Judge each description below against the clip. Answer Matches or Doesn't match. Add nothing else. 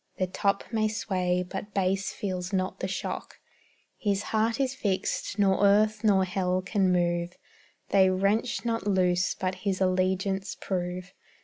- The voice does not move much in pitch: Matches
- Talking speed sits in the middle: Matches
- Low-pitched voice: Doesn't match